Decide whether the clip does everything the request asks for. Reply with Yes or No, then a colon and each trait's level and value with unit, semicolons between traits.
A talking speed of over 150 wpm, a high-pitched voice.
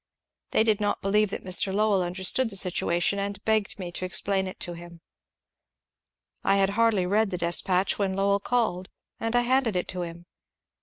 Yes: average, 190 wpm; high, 195 Hz